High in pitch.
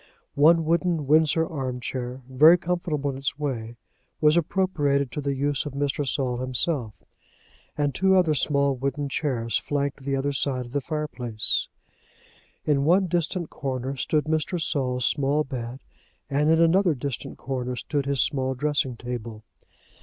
No: medium, 140 Hz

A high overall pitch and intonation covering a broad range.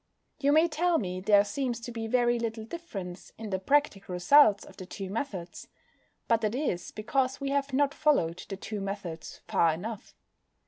Yes: high, 225 Hz; wide, 6.2 semitones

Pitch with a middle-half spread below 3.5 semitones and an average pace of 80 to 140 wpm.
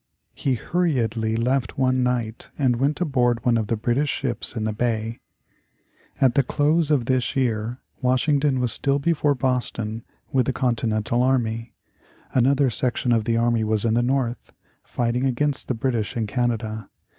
No: narrow, 2.6 semitones; average, 160 wpm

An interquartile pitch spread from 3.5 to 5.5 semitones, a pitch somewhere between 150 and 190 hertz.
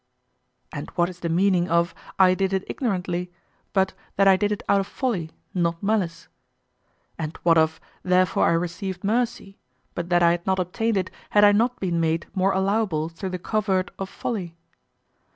No: narrow, 2.5 semitones; medium, 185 Hz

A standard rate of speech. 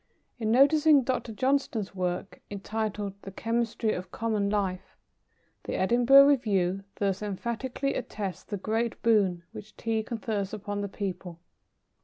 No: slow, 130 wpm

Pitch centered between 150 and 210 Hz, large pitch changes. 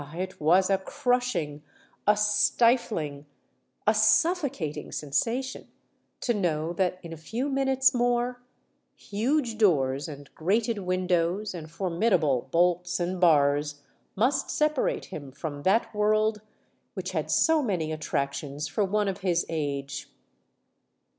Yes: medium, 185 Hz; wide, 6.6 semitones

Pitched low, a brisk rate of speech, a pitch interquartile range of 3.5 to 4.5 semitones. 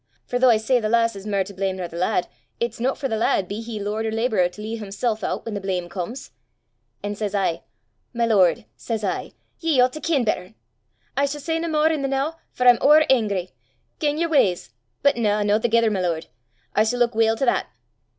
No: high, 220 Hz; fast, 230 wpm; average, 4.2 semitones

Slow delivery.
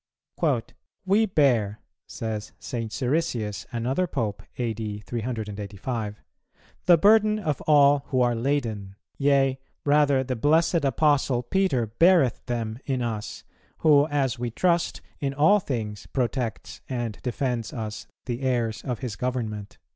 Yes: slow, 125 wpm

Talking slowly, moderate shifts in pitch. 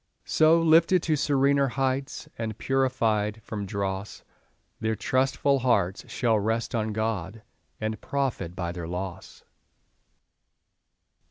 Yes: slow, 110 wpm; average, 5.0 semitones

